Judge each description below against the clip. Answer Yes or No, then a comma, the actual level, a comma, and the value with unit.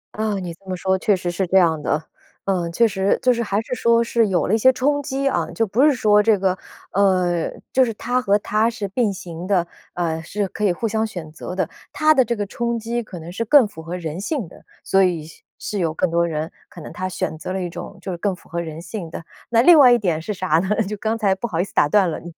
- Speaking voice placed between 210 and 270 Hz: No, high, 195 Hz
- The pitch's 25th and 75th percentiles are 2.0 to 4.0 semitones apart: No, average, 4.6 semitones